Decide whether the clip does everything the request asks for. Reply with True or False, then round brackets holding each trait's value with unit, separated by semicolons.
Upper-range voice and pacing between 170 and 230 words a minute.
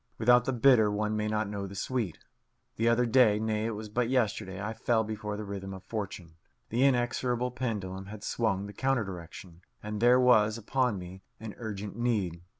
False (110 Hz; 190 wpm)